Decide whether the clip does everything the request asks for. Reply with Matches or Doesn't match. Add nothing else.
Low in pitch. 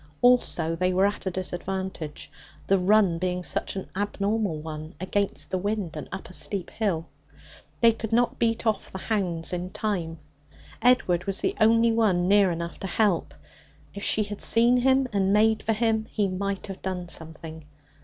Doesn't match